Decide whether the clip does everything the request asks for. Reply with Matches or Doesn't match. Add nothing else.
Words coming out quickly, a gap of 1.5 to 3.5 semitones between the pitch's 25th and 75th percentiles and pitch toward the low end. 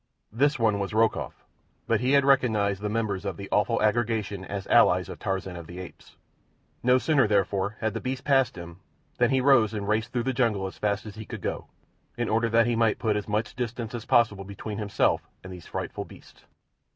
Matches